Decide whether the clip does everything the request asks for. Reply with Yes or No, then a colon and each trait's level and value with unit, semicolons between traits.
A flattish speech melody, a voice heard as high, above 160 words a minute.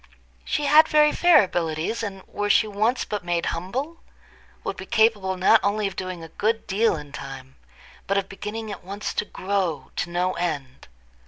No: average, 4.0 semitones; high, 195 Hz; average, 180 wpm